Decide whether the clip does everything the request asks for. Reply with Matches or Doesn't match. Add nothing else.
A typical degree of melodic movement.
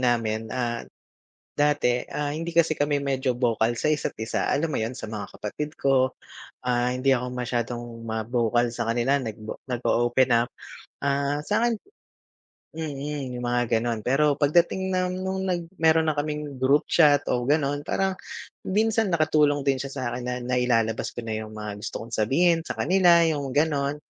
Matches